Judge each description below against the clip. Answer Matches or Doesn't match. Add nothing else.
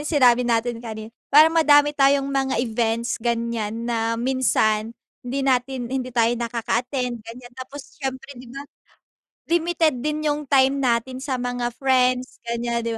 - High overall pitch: Matches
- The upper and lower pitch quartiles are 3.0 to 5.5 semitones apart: Doesn't match